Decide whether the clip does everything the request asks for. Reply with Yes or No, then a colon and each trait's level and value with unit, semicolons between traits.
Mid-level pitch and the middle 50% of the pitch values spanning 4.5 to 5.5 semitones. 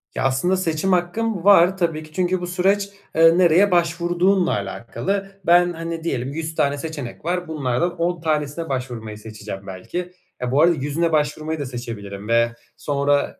Yes: medium, 160 Hz; average, 5.0 semitones